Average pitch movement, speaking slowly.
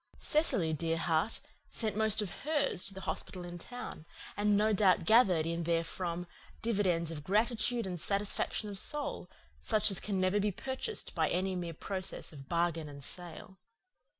No: average, 4.1 semitones; average, 165 wpm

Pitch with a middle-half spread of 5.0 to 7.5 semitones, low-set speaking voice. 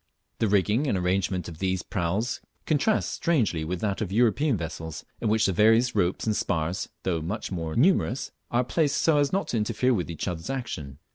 Yes: wide, 5.6 semitones; low, 105 Hz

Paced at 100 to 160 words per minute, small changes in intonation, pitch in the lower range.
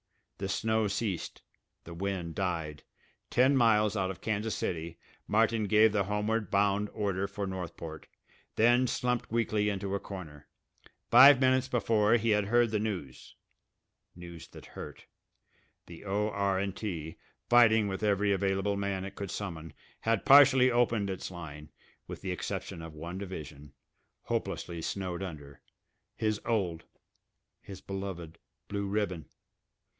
No: slow, 135 wpm; average, 3.6 semitones; low, 100 Hz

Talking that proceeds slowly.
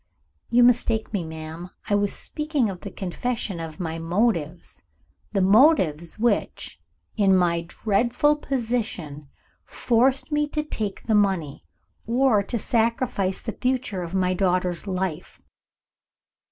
Yes: slow, 125 wpm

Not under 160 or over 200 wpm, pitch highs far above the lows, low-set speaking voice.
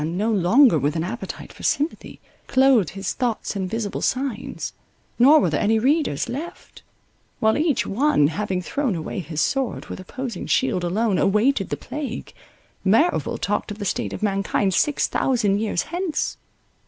No: average, 165 wpm; wide, 6.0 semitones; high, 220 Hz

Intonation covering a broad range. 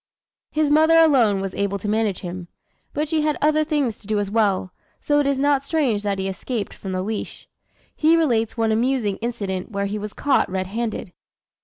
Yes: wide, 6.4 semitones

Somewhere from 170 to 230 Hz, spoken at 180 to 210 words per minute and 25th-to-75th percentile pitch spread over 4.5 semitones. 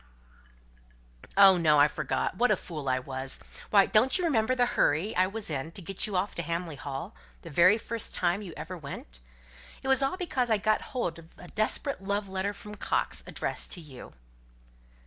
Yes: high, 190 Hz; average, 195 wpm; average, 5.1 semitones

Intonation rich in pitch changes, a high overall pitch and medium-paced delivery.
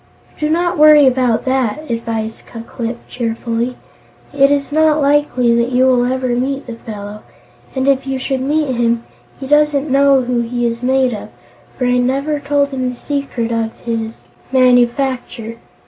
No: average, 3.0 semitones; very high, 255 Hz; average, 160 wpm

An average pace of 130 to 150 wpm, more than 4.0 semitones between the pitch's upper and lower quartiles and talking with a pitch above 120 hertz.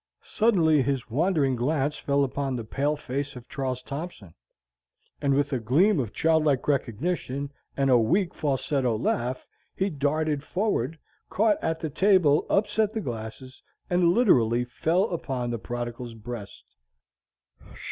Yes: slow, 135 wpm; average, 4.7 semitones; medium, 140 Hz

